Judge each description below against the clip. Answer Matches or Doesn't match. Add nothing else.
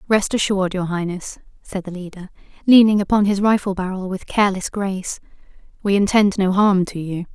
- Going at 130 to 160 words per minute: Doesn't match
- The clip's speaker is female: Matches